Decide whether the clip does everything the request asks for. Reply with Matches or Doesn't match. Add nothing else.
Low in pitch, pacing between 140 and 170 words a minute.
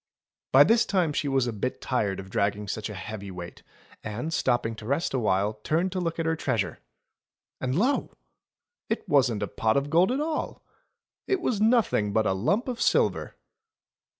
Doesn't match